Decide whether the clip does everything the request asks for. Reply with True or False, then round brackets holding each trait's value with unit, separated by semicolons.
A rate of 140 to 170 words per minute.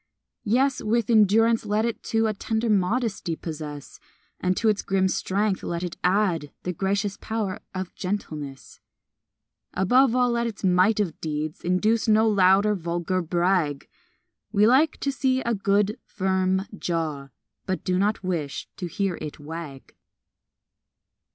True (145 wpm)